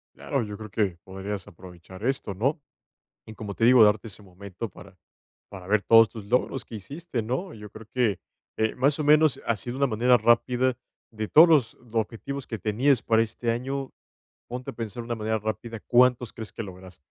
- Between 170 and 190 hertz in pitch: No, low, 115 Hz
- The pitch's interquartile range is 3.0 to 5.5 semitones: Yes, average, 3.4 semitones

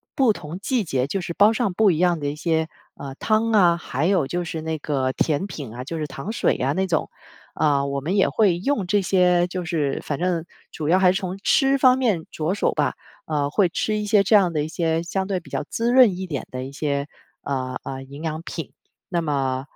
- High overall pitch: No, medium, 170 Hz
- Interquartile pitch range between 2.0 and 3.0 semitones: No, average, 5.1 semitones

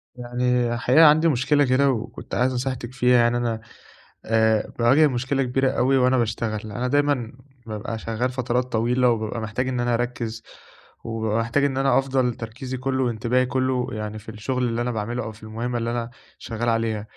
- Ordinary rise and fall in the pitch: No, narrow, 2.2 semitones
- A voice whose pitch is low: Yes, low, 120 Hz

